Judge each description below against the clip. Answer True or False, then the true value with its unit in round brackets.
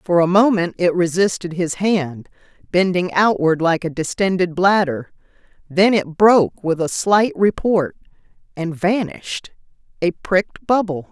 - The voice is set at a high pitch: False (180 Hz)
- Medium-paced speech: False (130 wpm)